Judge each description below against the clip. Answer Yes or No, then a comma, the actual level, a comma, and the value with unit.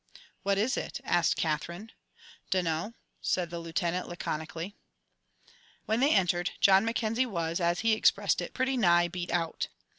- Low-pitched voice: No, medium, 180 Hz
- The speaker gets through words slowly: No, average, 145 wpm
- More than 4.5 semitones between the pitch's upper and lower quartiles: No, average, 4.2 semitones